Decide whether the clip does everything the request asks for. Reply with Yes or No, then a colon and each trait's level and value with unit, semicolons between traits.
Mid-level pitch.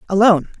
No: high, 195 Hz